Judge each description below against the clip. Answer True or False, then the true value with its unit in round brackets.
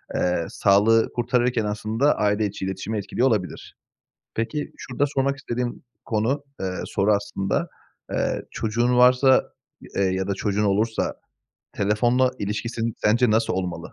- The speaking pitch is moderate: False (110 Hz)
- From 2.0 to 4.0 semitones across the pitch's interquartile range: True (3.5 semitones)